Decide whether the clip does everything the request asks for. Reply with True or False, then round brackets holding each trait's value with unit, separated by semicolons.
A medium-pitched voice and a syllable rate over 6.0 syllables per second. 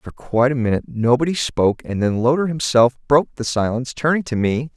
False (130 Hz; 6.2 syllables/s)